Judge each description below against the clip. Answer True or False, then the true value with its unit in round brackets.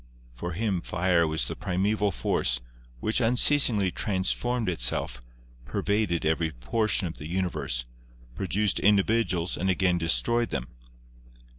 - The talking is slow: True (120 wpm)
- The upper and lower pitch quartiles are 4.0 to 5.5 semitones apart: True (4.3 semitones)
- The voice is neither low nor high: False (95 Hz)